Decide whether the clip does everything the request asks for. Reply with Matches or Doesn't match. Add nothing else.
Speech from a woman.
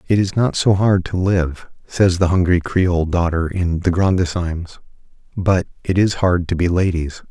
Doesn't match